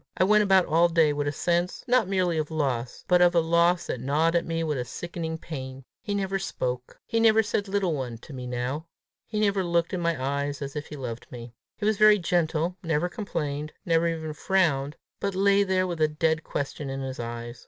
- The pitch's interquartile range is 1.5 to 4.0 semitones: No, average, 4.6 semitones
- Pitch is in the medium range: Yes, medium, 165 Hz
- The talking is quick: Yes, fast, 220 wpm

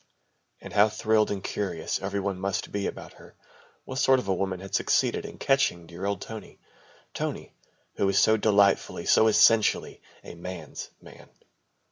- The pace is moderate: Yes, average, 165 wpm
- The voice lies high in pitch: No, low, 100 Hz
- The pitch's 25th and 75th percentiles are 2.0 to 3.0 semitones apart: Yes, narrow, 2.5 semitones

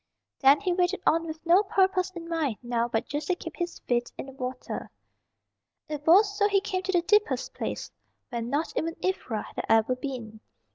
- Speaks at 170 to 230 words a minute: Yes, average, 195 wpm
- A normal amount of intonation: No, wide, 6.6 semitones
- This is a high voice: Yes, very high, 325 Hz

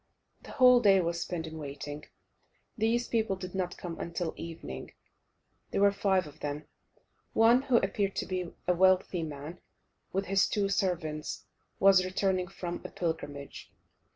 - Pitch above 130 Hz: Yes, medium, 185 Hz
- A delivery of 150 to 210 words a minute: Yes, average, 155 wpm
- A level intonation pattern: No, average, 3.3 semitones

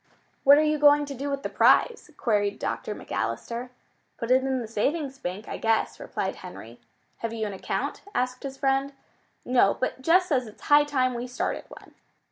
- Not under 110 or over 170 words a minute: No, average, 190 wpm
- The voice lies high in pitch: Yes, very high, 260 Hz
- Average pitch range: Yes, average, 3.6 semitones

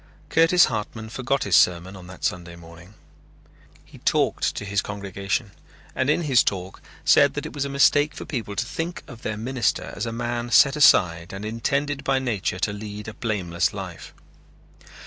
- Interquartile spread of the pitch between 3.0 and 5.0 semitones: No, wide, 5.6 semitones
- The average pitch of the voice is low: Yes, low, 110 Hz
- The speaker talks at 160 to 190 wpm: Yes, average, 180 wpm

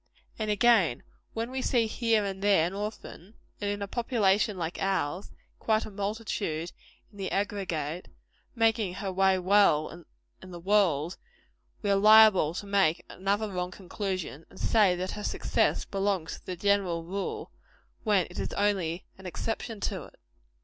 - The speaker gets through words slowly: No, average, 165 wpm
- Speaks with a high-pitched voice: Yes, high, 195 Hz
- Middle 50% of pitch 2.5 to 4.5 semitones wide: Yes, average, 2.8 semitones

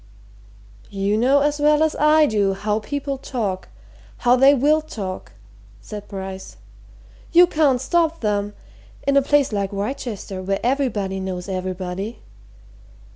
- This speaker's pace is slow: Yes, slow, 130 wpm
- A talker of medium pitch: No, high, 220 Hz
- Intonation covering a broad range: Yes, wide, 6.5 semitones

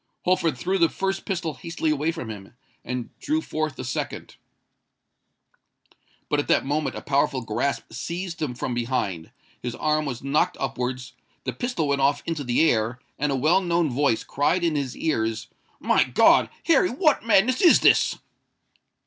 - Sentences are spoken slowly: No, average, 155 wpm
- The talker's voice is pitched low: No, medium, 145 Hz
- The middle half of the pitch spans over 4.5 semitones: Yes, average, 5.1 semitones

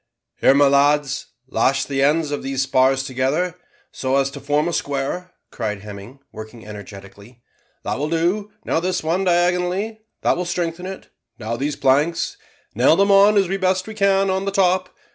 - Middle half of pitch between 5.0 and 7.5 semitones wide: Yes, wide, 5.5 semitones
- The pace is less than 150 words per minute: No, average, 175 wpm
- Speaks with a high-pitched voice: No, medium, 150 Hz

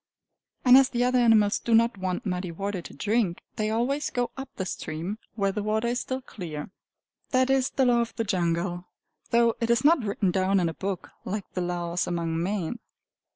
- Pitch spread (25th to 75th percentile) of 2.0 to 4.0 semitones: No, average, 4.9 semitones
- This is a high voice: Yes, high, 205 Hz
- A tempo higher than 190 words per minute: Yes, average, 200 wpm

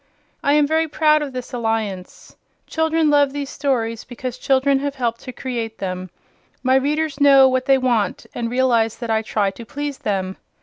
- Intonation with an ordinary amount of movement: Yes, average, 4.0 semitones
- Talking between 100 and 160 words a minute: No, average, 180 wpm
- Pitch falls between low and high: No, very high, 260 Hz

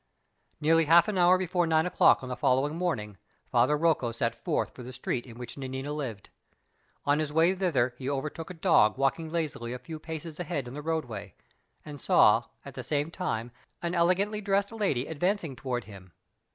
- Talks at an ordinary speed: Yes, average, 190 wpm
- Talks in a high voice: No, medium, 150 Hz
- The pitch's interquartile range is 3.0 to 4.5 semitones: No, average, 5.2 semitones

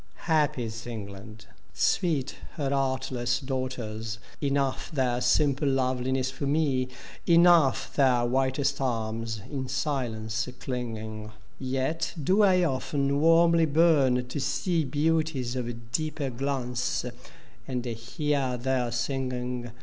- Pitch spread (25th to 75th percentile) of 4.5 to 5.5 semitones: No, average, 3.1 semitones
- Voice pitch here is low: Yes, low, 130 Hz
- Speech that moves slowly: Yes, slow, 110 wpm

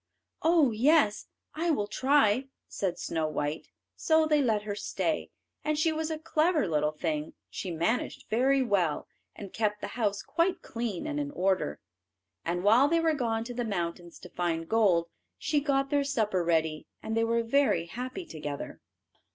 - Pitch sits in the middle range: No, high, 225 Hz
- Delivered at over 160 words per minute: Yes, average, 170 wpm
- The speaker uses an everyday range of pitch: No, wide, 8.4 semitones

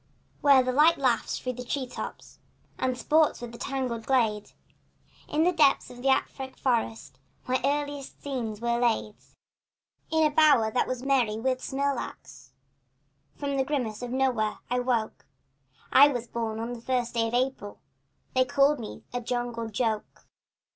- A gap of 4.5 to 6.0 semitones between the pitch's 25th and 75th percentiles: No, average, 2.9 semitones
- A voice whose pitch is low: No, very high, 250 Hz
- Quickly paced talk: No, average, 170 wpm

